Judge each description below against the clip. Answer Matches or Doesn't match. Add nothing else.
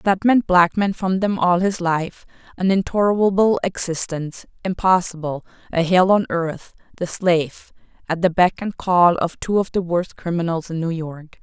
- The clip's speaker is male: Doesn't match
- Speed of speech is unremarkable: Matches